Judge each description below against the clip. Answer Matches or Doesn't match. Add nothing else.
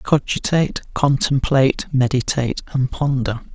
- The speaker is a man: Matches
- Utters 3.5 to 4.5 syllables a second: Matches